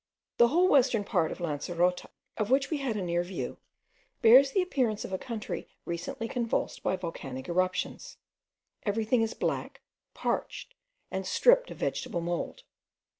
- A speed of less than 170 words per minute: Yes, average, 150 wpm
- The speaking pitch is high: Yes, high, 215 Hz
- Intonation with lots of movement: Yes, wide, 6.5 semitones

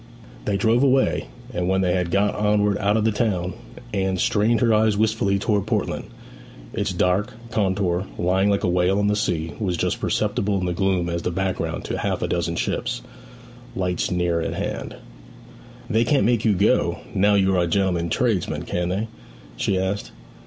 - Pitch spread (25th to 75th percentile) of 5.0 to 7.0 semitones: No, narrow, 2.6 semitones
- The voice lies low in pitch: Yes, low, 100 Hz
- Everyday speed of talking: Yes, average, 185 wpm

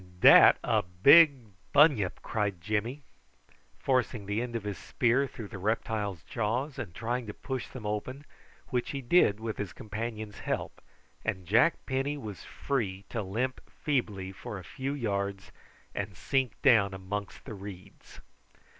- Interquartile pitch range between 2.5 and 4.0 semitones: No, average, 4.5 semitones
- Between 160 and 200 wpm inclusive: No, average, 150 wpm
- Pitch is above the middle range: No, low, 110 Hz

